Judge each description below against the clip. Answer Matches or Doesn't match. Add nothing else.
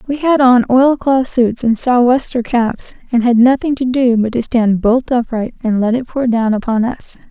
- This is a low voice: Doesn't match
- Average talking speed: Doesn't match